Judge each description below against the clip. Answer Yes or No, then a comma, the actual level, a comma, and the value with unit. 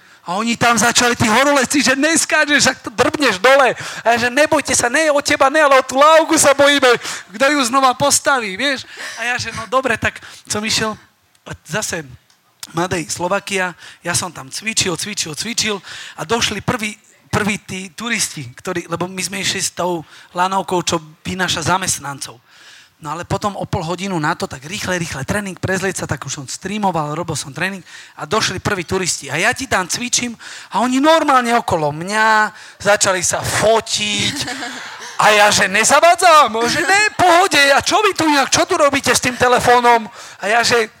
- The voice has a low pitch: No, high, 215 Hz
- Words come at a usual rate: No, fast, 185 wpm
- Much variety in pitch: Yes, wide, 6.8 semitones